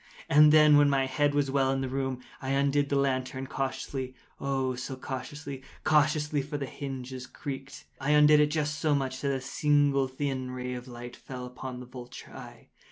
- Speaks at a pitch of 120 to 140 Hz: Yes, low, 135 Hz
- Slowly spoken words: No, average, 165 wpm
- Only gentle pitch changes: Yes, narrow, 1.9 semitones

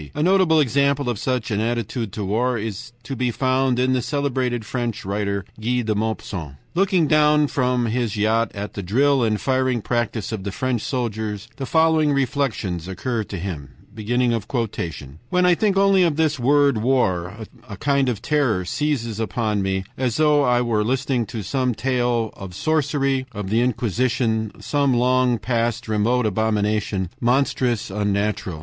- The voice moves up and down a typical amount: Yes, average, 4.0 semitones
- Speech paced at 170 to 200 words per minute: No, average, 160 wpm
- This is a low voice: Yes, low, 120 Hz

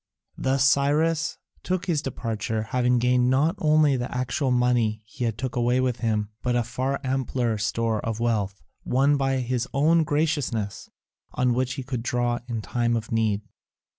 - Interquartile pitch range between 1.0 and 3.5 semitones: Yes, average, 2.8 semitones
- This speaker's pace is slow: No, average, 165 wpm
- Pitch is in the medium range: No, low, 125 Hz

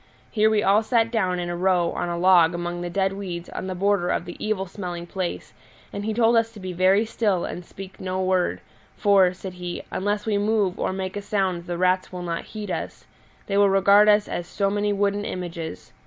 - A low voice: No, high, 190 Hz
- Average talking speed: No, fast, 225 wpm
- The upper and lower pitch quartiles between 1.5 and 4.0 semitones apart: Yes, narrow, 2.5 semitones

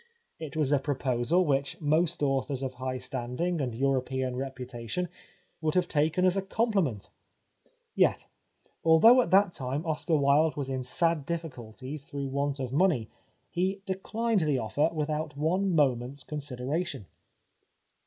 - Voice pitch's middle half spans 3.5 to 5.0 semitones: Yes, average, 4.3 semitones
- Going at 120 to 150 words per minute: Yes, average, 145 wpm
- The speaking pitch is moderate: Yes, medium, 145 Hz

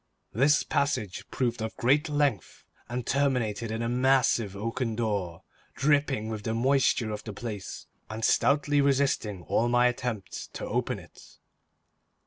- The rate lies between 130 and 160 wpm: Yes, average, 140 wpm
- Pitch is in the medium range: No, low, 120 Hz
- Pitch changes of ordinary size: Yes, average, 3.9 semitones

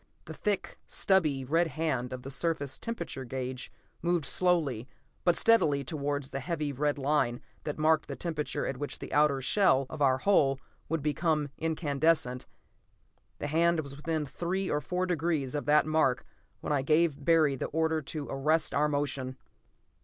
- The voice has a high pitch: No, medium, 150 Hz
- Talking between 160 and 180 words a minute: Yes, average, 165 wpm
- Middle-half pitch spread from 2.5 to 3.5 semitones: Yes, average, 3.1 semitones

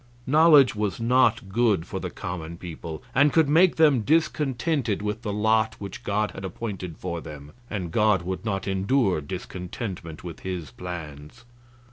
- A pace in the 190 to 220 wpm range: No, average, 155 wpm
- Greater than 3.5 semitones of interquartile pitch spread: Yes, wide, 5.4 semitones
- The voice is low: Yes, low, 105 Hz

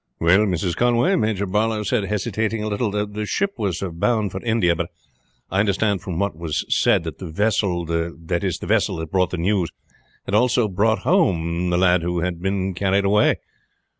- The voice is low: Yes, very low, 95 Hz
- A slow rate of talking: No, average, 190 wpm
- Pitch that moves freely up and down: No, average, 3.6 semitones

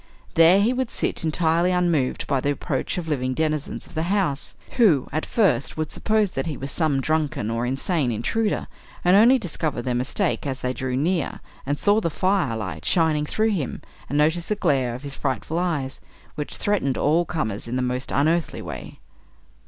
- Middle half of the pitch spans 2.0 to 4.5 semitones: No, average, 5.2 semitones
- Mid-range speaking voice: Yes, medium, 155 Hz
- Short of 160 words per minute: No, average, 190 wpm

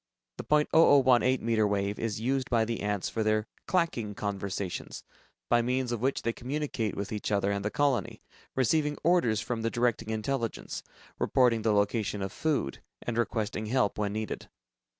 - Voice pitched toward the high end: No, low, 115 Hz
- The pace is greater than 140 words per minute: Yes, average, 165 wpm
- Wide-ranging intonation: No, average, 3.7 semitones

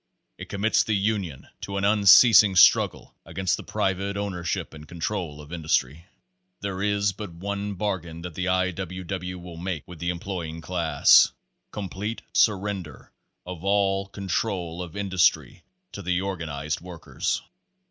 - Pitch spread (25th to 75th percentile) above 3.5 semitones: No, average, 2.8 semitones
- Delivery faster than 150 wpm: No, average, 145 wpm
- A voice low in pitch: Yes, very low, 95 Hz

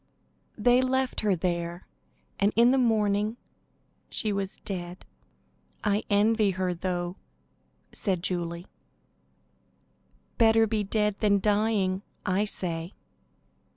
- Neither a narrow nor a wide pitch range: Yes, average, 3.1 semitones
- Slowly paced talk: Yes, slow, 105 wpm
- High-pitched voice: Yes, high, 200 Hz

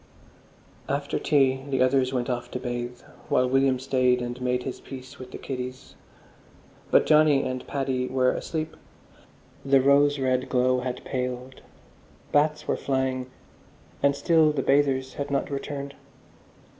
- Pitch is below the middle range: Yes, low, 130 Hz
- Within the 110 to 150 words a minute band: Yes, average, 145 wpm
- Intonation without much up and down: Yes, narrow, 1.7 semitones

